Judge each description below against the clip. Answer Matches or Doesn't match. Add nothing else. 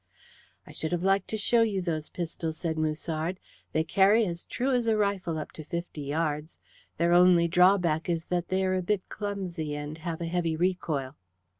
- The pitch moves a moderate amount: Matches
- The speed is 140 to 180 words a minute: Doesn't match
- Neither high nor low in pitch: Matches